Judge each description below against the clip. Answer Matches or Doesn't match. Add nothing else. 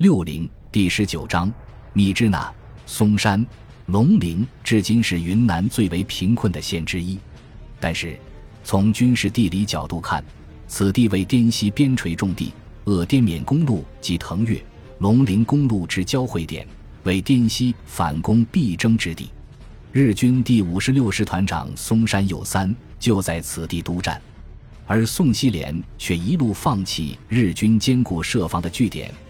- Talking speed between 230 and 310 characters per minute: Doesn't match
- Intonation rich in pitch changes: Doesn't match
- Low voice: Matches